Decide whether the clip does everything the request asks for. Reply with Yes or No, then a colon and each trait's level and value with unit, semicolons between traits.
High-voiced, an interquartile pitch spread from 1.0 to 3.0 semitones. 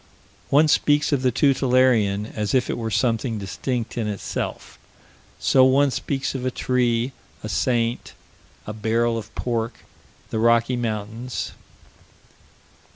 No: low, 120 Hz; narrow, 2.6 semitones